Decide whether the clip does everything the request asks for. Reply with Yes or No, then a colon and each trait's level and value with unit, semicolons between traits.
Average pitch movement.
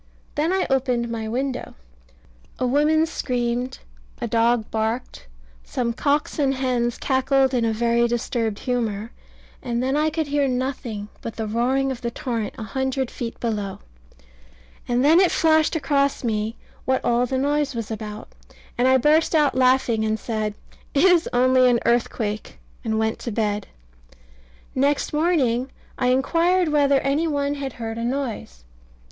Yes: average, 3.4 semitones